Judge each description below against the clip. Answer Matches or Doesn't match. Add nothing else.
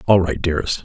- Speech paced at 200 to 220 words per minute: Matches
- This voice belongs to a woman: Doesn't match